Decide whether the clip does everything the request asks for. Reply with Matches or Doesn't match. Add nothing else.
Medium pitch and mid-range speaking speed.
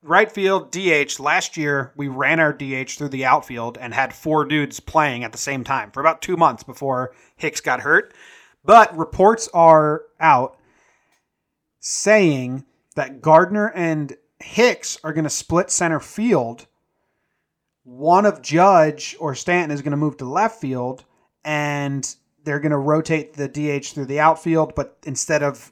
Matches